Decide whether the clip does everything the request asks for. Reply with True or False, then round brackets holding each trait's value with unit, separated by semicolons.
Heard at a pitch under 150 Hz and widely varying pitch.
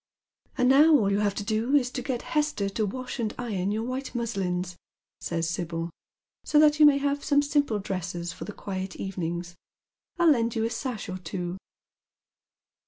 False (220 Hz; 6.3 semitones)